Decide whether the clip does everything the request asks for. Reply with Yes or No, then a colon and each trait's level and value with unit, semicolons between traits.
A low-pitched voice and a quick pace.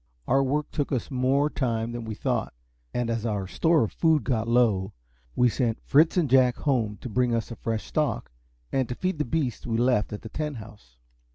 Yes: low, 125 Hz; fast, 210 wpm